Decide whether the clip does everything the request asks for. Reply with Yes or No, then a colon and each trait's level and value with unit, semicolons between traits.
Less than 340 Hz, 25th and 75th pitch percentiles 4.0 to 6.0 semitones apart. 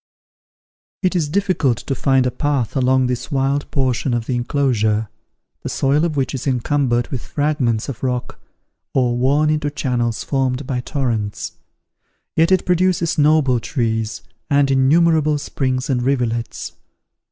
No: low, 135 Hz; average, 3.1 semitones